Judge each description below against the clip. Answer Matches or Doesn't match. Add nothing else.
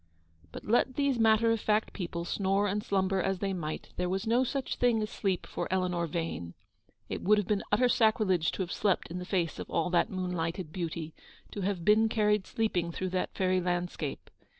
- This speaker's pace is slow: Doesn't match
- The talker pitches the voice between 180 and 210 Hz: Matches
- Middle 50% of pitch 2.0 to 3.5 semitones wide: Matches